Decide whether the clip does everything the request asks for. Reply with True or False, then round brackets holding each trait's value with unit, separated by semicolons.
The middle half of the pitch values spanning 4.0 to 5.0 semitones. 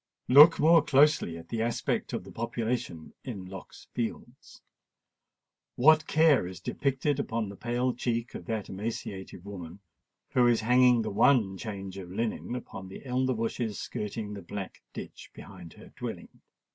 True (4.5 semitones)